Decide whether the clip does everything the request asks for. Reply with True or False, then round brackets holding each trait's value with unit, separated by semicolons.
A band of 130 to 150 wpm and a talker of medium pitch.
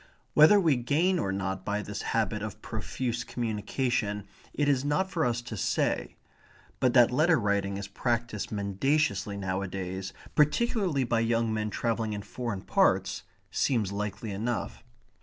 False (145 wpm; 115 Hz)